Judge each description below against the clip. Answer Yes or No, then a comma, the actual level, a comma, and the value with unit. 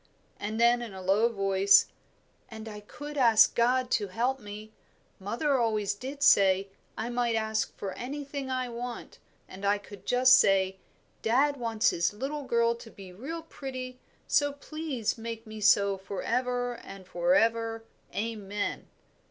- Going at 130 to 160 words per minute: Yes, average, 155 wpm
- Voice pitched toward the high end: Yes, high, 230 Hz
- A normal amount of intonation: Yes, average, 3.8 semitones